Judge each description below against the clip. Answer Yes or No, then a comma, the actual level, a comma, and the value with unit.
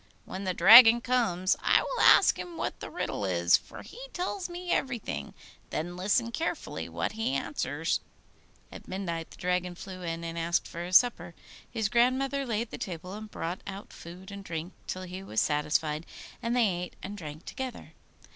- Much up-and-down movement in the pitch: Yes, wide, 5.7 semitones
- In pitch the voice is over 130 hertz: Yes, medium, 185 Hz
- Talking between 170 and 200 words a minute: Yes, average, 180 wpm